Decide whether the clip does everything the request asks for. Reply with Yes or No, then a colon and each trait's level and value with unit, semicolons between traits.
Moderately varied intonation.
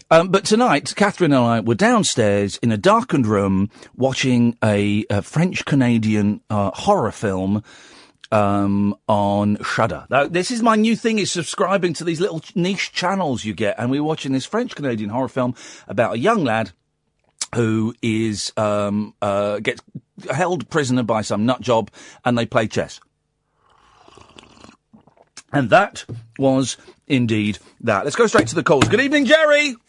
No: wide, 8.4 semitones